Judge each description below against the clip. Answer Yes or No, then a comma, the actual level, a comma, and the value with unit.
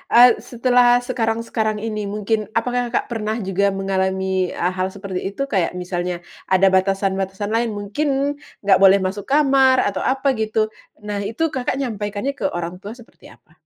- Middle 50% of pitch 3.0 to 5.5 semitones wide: Yes, average, 3.7 semitones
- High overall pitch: Yes, high, 210 Hz